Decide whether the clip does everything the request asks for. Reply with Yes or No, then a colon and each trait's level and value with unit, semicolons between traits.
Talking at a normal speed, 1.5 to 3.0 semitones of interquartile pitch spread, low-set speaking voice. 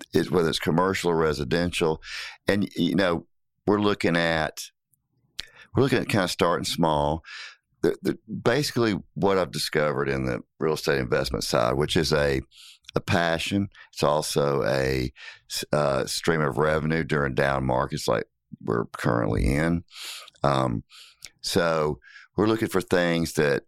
No: average, 145 wpm; average, 5.0 semitones; very low, 80 Hz